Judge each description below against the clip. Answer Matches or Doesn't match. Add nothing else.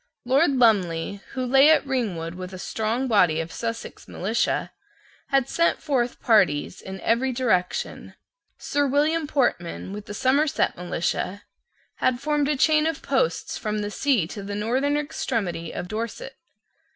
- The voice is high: Matches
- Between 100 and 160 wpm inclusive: Matches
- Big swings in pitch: Matches